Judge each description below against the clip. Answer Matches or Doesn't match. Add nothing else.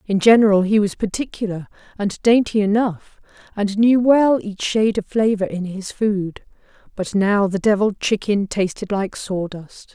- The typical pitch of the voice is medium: Doesn't match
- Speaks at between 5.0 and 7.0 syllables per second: Doesn't match